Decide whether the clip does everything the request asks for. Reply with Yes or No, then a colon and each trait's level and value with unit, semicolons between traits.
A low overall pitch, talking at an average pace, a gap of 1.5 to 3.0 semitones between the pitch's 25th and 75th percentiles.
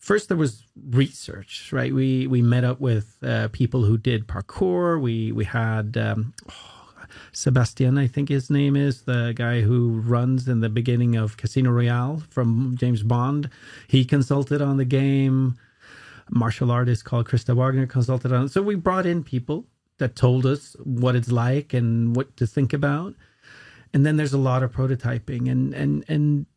Yes: low, 125 Hz; average, 180 wpm; narrow, 2.6 semitones